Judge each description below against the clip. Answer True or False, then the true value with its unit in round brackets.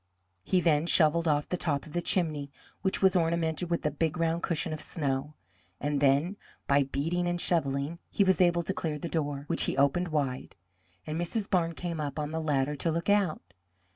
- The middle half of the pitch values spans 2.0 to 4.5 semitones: True (3.1 semitones)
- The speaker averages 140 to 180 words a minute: False (200 wpm)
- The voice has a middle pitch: True (160 Hz)